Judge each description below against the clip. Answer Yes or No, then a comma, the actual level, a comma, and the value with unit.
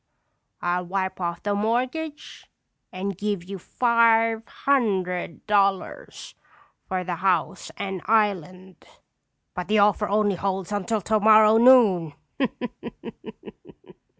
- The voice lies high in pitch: Yes, high, 200 Hz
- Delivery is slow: Yes, slow, 100 wpm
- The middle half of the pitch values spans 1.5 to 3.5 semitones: Yes, average, 3.1 semitones